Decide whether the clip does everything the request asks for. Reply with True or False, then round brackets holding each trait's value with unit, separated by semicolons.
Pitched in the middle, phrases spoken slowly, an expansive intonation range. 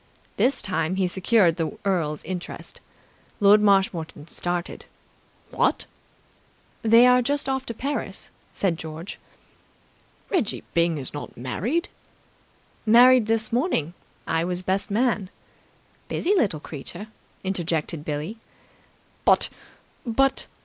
False (195 Hz; 110 wpm; 5.9 semitones)